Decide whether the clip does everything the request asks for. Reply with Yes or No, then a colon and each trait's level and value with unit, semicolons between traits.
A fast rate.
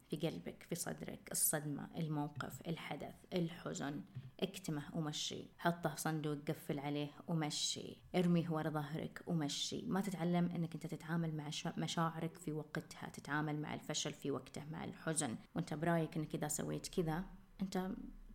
Yes: fast, 140 wpm